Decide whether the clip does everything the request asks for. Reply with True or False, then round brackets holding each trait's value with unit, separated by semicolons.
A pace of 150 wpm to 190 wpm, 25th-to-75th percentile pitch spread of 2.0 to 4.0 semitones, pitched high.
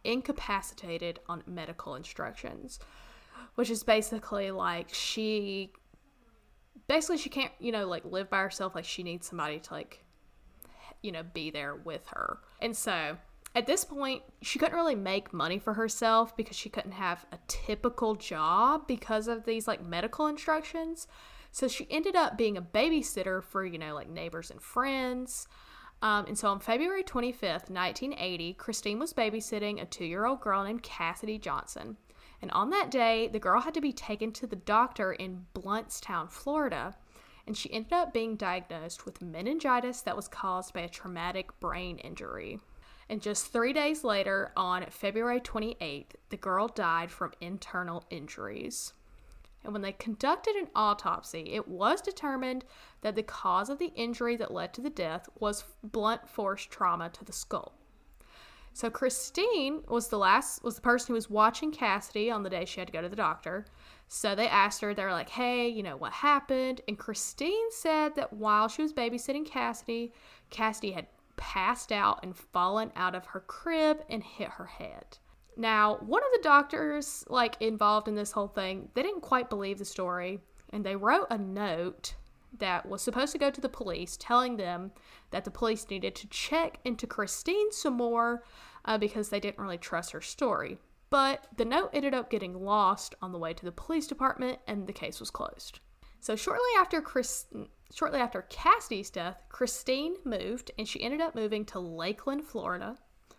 False (175 wpm; 4.9 semitones; 220 Hz)